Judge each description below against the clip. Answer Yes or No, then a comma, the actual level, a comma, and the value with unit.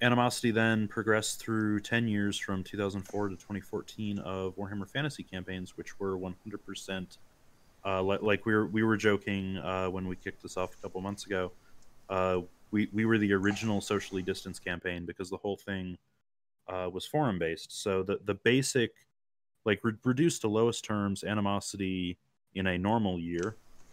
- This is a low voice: Yes, low, 100 Hz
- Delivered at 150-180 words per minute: Yes, average, 170 wpm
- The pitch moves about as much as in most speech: No, narrow, 2.3 semitones